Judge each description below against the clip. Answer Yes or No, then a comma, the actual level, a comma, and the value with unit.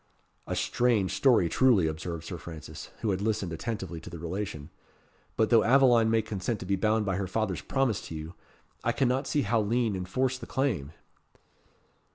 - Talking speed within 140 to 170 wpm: No, average, 180 wpm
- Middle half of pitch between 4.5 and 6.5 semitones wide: Yes, average, 5.2 semitones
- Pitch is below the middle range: Yes, low, 105 Hz